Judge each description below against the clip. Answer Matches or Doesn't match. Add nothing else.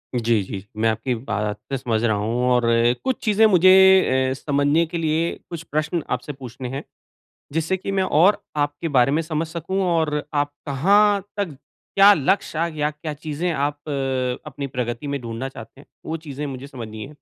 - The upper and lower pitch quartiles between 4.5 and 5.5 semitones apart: Matches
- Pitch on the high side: Doesn't match